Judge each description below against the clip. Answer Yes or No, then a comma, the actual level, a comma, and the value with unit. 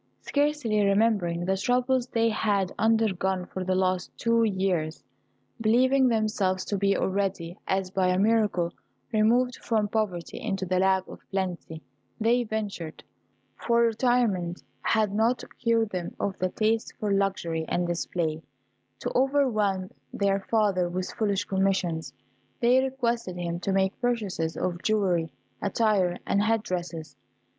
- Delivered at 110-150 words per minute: Yes, slow, 135 wpm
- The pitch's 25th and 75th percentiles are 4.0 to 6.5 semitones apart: No, average, 3.6 semitones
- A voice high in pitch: Yes, high, 200 Hz